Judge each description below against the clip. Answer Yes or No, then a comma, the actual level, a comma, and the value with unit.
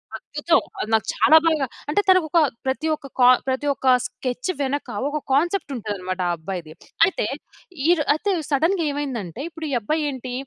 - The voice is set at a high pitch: Yes, very high, 280 Hz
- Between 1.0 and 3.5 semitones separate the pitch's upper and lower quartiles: No, average, 4.5 semitones